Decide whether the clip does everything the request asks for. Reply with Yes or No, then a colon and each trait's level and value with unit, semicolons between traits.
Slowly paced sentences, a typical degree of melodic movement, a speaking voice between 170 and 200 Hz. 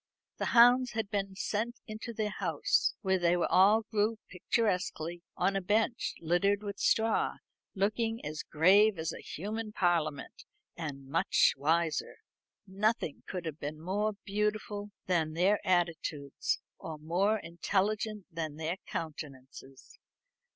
Yes: slow, 130 wpm; average, 4.6 semitones; high, 190 Hz